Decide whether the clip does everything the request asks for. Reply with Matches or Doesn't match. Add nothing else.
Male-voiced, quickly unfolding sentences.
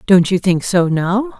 Doesn't match